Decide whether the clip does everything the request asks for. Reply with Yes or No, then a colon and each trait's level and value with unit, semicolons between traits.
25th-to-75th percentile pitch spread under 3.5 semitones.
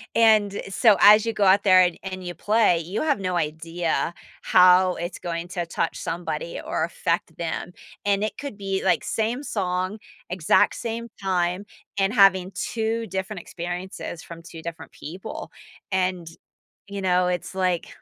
Yes: average, 3.0 semitones